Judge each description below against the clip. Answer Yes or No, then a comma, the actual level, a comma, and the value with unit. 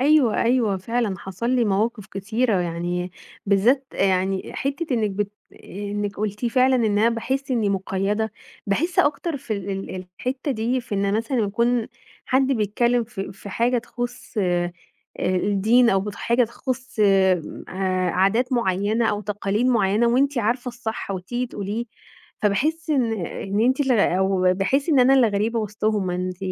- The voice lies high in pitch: Yes, high, 220 Hz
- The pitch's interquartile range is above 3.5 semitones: Yes, average, 4.0 semitones